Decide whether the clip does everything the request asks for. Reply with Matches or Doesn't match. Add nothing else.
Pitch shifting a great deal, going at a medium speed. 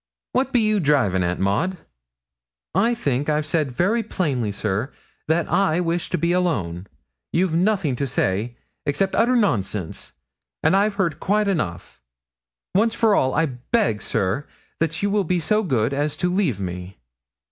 Matches